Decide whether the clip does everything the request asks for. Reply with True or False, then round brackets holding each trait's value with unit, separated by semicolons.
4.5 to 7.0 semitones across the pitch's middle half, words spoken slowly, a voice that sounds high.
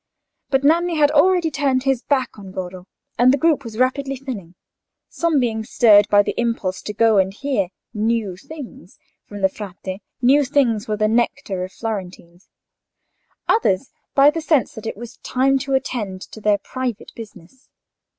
False (5.2 semitones; 170 wpm; 235 Hz)